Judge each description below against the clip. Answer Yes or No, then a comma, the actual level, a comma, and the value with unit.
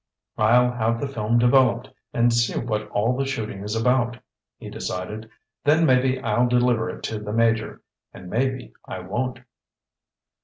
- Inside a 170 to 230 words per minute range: No, average, 155 wpm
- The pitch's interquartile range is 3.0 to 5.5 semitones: No, narrow, 2.6 semitones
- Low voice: Yes, low, 120 Hz